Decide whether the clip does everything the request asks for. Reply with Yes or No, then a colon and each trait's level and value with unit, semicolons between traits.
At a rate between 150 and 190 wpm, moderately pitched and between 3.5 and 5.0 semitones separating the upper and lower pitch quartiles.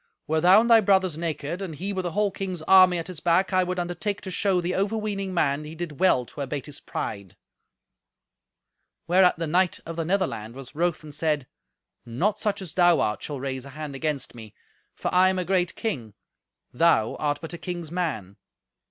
No: fast, 205 wpm; medium, 170 Hz; average, 4.2 semitones